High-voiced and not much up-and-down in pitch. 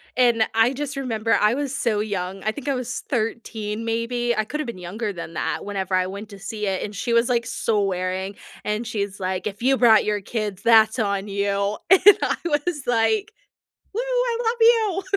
No: high, 225 Hz; average, 4.1 semitones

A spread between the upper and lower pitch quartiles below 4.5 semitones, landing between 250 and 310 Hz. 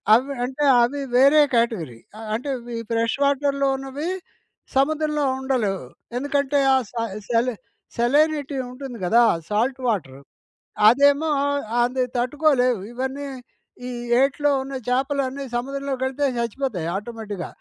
Yes: average, 3.0 semitones; very high, 265 Hz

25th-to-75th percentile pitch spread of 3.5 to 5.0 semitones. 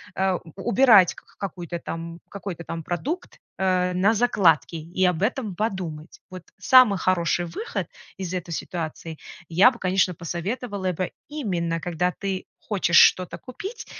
No: average, 3.1 semitones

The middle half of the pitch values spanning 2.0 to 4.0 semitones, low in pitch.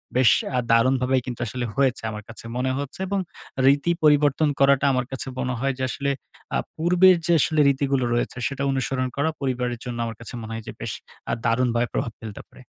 Yes: narrow, 2.5 semitones; low, 130 Hz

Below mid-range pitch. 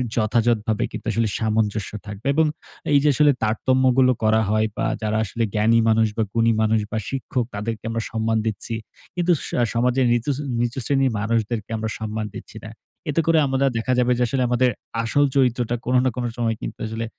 Yes: low, 115 Hz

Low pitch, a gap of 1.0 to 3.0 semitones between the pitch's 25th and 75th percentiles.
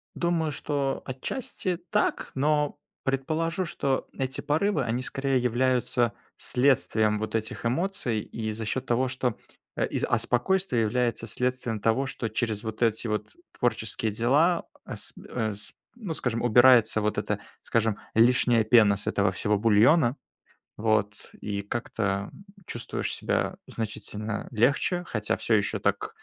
No: low, 120 Hz; average, 3.8 semitones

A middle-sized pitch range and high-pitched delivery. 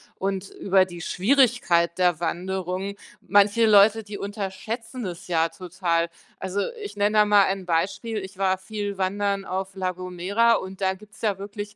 No: narrow, 2.0 semitones; high, 195 Hz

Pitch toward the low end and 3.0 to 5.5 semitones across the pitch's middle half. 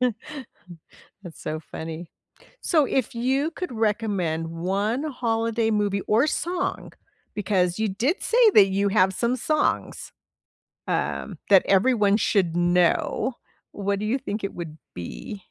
No: high, 210 Hz; average, 5.1 semitones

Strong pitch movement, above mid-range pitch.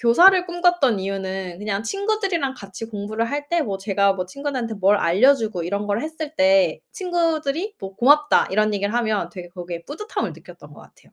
Yes: wide, 7.8 semitones; high, 230 Hz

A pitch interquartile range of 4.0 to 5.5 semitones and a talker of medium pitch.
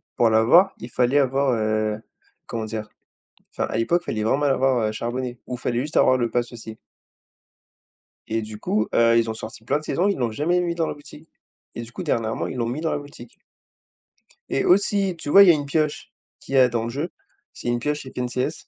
No: average, 4.5 semitones; low, 125 Hz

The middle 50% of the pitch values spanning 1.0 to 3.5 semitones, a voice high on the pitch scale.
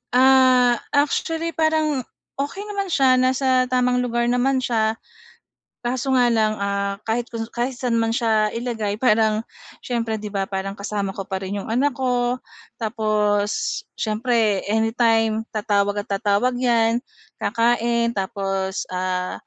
Yes: average, 3.2 semitones; high, 230 Hz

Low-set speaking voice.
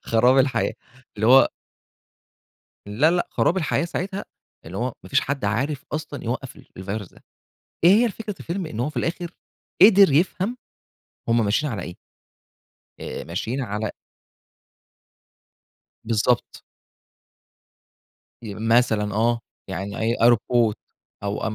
Yes: low, 120 Hz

